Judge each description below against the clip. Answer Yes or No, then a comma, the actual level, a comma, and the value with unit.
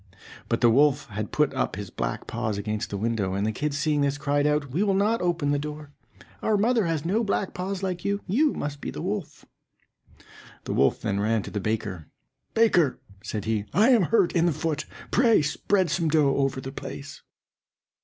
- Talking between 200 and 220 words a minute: Yes, fast, 205 wpm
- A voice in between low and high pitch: Yes, medium, 150 Hz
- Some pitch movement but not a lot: No, wide, 8.1 semitones